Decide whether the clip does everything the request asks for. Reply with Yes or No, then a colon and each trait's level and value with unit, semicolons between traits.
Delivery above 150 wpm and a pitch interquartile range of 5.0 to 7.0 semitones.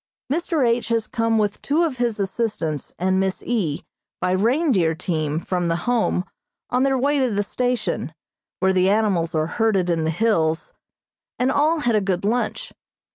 Yes: average, 175 wpm; wide, 5.5 semitones